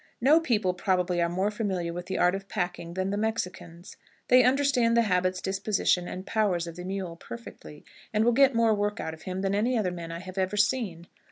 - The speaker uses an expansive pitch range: No, average, 3.8 semitones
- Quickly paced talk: Yes, fast, 215 wpm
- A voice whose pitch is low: No, high, 195 Hz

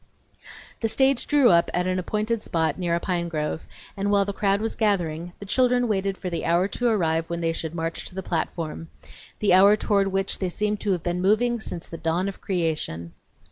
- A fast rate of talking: Yes, fast, 215 wpm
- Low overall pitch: No, medium, 185 Hz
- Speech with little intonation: No, average, 3.7 semitones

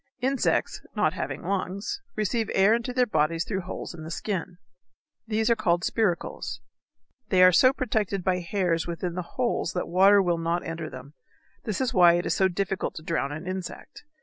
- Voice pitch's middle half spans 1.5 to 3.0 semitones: No, average, 3.8 semitones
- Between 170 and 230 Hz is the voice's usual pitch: Yes, medium, 185 Hz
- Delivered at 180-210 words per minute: Yes, average, 185 wpm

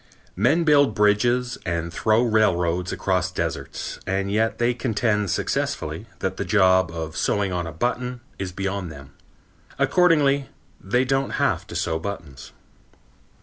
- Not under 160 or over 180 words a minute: No, average, 140 wpm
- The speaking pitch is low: Yes, low, 100 Hz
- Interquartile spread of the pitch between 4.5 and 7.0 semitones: Yes, wide, 5.5 semitones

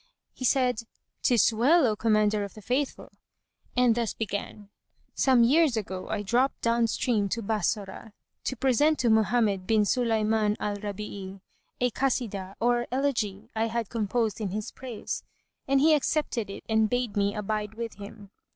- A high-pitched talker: Yes, high, 220 Hz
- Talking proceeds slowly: No, average, 160 wpm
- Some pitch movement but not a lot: Yes, average, 3.0 semitones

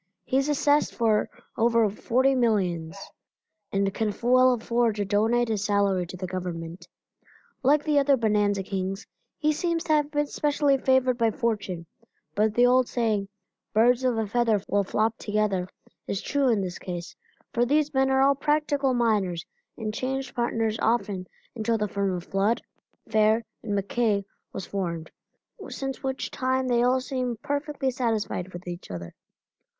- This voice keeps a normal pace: Yes, average, 165 wpm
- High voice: Yes, high, 225 Hz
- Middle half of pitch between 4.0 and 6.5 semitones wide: Yes, average, 4.6 semitones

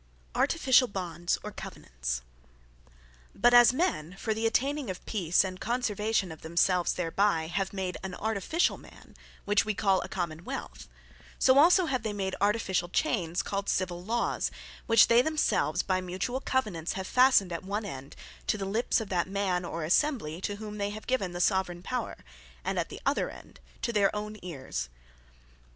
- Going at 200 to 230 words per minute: No, average, 170 wpm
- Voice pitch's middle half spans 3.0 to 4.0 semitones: No, average, 4.4 semitones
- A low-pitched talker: No, high, 195 Hz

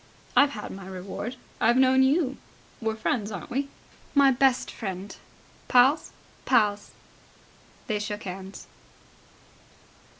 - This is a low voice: No, high, 225 Hz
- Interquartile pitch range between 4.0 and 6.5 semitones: Yes, average, 4.7 semitones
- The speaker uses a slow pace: Yes, slow, 110 wpm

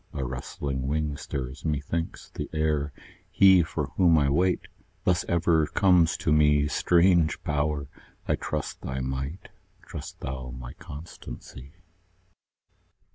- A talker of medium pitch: No, very low, 75 Hz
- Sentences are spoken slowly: Yes, slow, 125 wpm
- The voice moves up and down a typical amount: Yes, average, 3.4 semitones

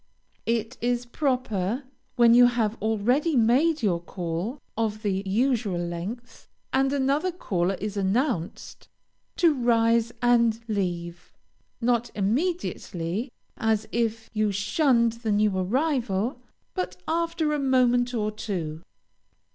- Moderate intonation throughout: Yes, average, 4.1 semitones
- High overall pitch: Yes, high, 230 Hz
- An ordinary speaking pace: No, slow, 115 wpm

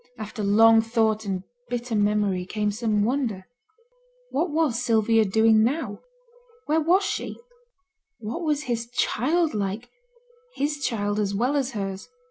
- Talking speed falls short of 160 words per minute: Yes, slow, 135 wpm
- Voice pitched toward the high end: Yes, high, 225 Hz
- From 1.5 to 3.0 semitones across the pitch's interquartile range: No, average, 4.1 semitones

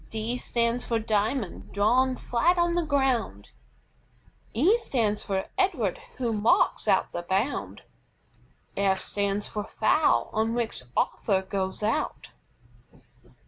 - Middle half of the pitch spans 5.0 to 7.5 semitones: No, average, 4.2 semitones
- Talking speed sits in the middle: No, slow, 120 wpm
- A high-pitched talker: Yes, high, 225 Hz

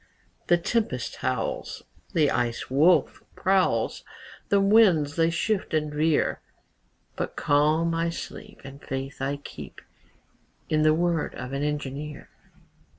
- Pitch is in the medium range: Yes, medium, 155 Hz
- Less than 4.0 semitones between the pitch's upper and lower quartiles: Yes, average, 3.2 semitones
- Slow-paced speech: Yes, slow, 125 wpm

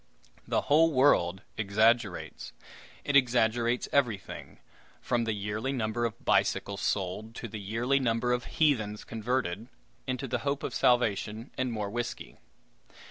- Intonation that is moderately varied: Yes, average, 3.0 semitones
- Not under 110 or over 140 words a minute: Yes, slow, 135 wpm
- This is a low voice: Yes, low, 115 Hz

